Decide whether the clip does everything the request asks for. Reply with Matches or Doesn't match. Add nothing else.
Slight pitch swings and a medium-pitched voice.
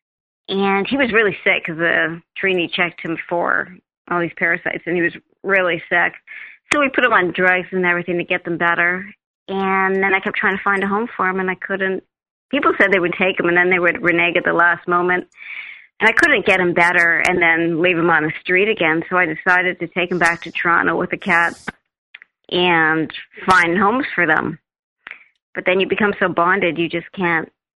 Matches